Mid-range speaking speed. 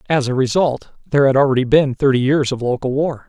No: fast, 220 wpm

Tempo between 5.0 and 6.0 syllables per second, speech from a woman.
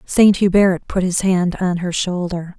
No: 4.0 syllables/s; female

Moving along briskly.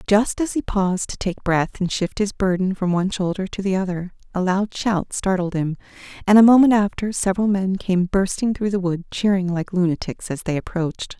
Yes: fast, 210 wpm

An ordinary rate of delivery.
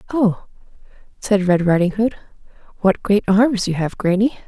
Yes: average, 150 wpm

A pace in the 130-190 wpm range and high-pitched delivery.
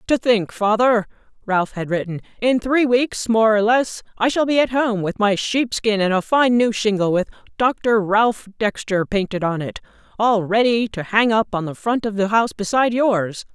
No: average, 200 wpm; high, 215 Hz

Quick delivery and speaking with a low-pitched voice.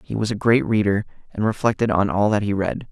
Yes: fast, 245 wpm; low, 105 Hz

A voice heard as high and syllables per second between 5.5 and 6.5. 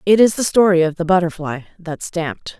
No: medium, 180 Hz; 5.6 syllables/s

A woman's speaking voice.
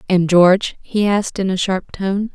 Yes: female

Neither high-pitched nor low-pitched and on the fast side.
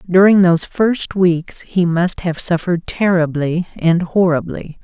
No: medium, 175 Hz; slow, 135 wpm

